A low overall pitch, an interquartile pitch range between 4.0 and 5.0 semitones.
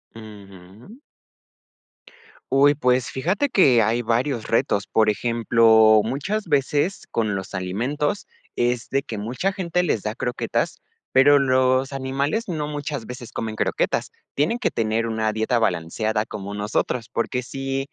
Yes: low, 120 Hz; average, 4.3 semitones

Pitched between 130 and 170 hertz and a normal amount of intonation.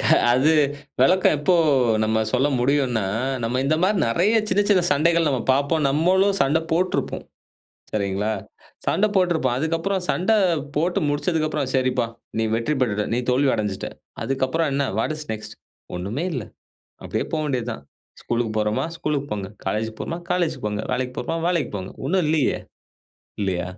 No: medium, 140 Hz; wide, 6.1 semitones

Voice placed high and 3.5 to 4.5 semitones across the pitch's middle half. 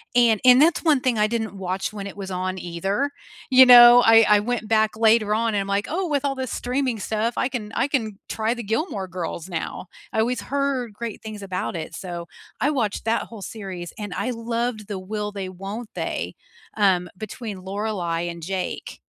Yes: high, 215 Hz; average, 3.8 semitones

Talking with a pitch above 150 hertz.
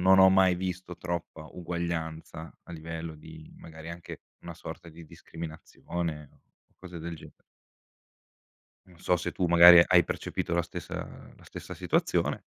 No: very low, 85 Hz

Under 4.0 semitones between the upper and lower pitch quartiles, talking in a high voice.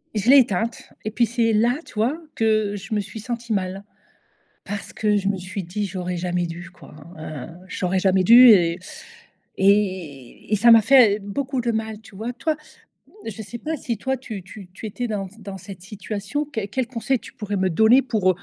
Yes: average, 3.6 semitones; high, 210 Hz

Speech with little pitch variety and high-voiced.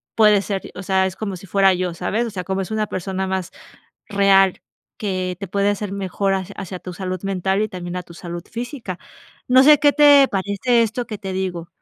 Yes: narrow, 2.3 semitones; high, 195 Hz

